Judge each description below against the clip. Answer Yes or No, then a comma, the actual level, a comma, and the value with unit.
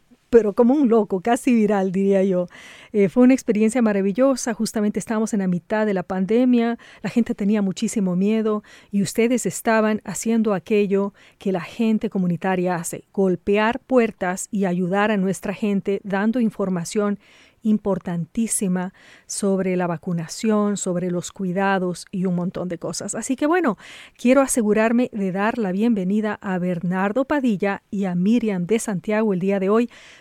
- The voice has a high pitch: Yes, high, 205 Hz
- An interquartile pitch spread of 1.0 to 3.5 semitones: Yes, average, 3.0 semitones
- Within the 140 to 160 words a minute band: Yes, average, 155 wpm